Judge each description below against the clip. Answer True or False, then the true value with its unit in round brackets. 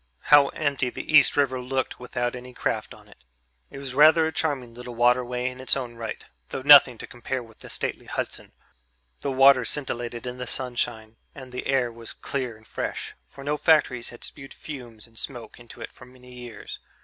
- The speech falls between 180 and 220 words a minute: True (195 wpm)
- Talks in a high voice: False (125 Hz)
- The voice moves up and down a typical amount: False (2.2 semitones)